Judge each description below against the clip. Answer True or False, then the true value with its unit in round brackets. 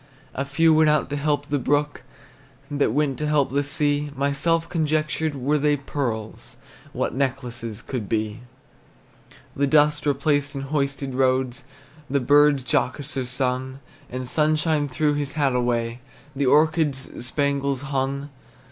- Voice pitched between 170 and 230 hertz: False (140 Hz)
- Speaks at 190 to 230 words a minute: False (140 wpm)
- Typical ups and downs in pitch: False (2.2 semitones)